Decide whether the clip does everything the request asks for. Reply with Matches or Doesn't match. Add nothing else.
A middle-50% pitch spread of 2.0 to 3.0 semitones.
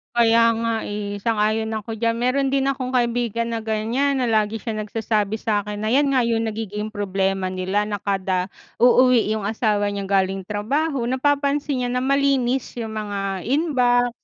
Doesn't match